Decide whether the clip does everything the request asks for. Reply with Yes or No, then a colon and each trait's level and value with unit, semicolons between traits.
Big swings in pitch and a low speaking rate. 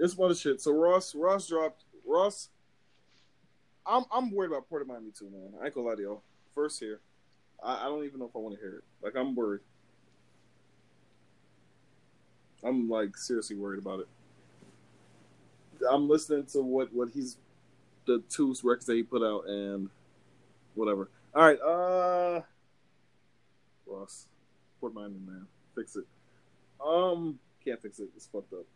No: wide, 7.3 semitones; average, 165 wpm